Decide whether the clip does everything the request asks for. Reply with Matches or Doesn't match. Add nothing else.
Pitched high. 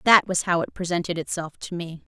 Doesn't match